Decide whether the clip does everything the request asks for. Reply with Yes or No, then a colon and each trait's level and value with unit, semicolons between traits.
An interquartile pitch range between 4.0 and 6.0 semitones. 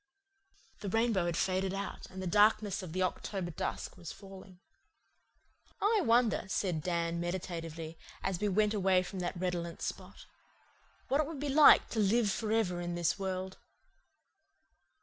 No: average, 3.4 semitones